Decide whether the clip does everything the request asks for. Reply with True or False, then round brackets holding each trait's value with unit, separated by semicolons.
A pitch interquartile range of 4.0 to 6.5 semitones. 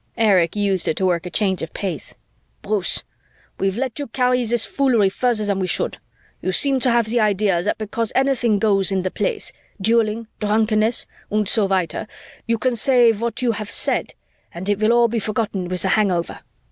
False (3.4 semitones)